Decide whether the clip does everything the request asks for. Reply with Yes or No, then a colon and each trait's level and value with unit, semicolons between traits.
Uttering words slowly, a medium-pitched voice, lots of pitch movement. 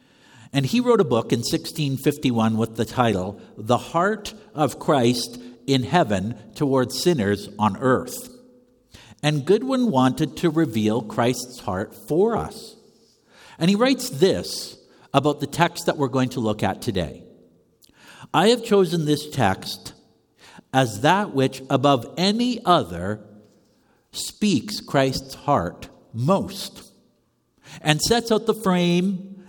Yes: slow, 130 wpm; medium, 145 Hz; wide, 7.8 semitones